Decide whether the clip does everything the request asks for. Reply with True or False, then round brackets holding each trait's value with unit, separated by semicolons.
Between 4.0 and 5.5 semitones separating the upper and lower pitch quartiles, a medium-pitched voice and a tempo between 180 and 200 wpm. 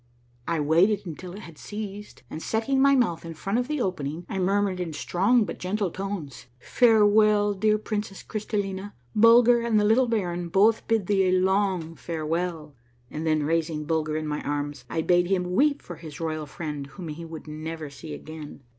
True (4.9 semitones; 180 Hz; 195 wpm)